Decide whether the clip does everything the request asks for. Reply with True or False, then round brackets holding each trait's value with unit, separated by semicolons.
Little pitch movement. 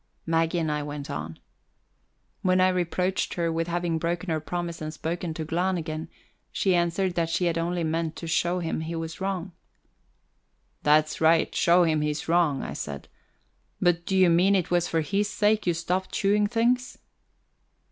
True (2.1 semitones)